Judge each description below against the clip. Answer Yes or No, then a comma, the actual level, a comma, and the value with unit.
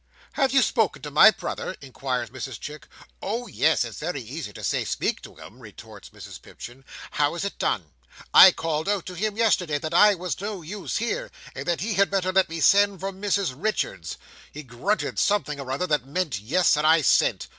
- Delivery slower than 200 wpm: No, fast, 205 wpm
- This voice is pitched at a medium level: Yes, medium, 170 Hz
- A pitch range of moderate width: No, wide, 6.1 semitones